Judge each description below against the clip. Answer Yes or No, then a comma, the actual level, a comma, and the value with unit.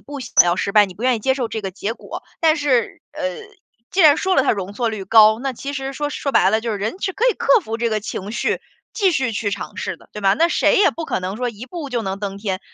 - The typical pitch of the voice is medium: No, high, 235 Hz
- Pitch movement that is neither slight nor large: No, wide, 5.7 semitones